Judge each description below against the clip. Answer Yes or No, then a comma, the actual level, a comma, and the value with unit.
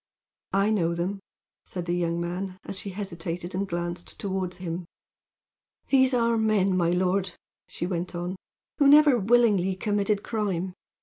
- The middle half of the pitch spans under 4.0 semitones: Yes, average, 3.0 semitones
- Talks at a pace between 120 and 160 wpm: Yes, average, 145 wpm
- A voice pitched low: No, high, 190 Hz